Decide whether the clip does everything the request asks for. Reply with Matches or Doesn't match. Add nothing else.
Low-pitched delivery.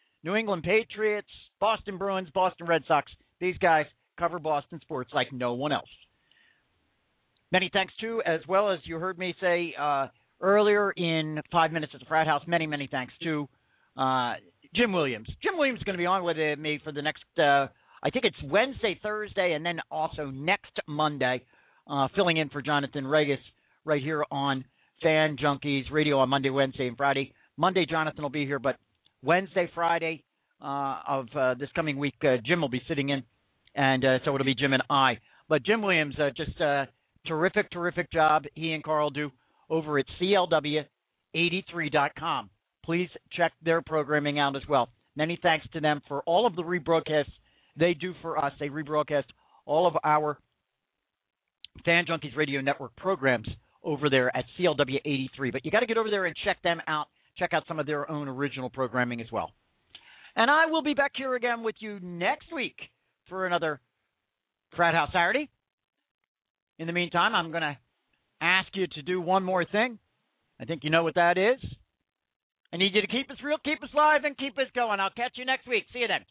Doesn't match